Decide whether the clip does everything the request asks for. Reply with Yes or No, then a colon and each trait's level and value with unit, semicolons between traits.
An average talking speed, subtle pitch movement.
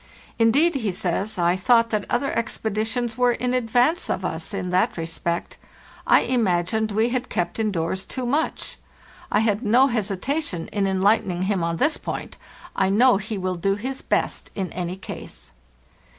No: average, 165 wpm; average, 4.7 semitones